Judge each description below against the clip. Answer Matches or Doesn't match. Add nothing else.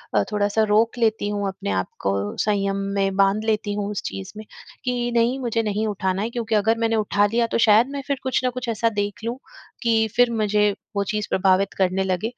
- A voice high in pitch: Matches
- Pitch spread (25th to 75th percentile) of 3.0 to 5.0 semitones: Doesn't match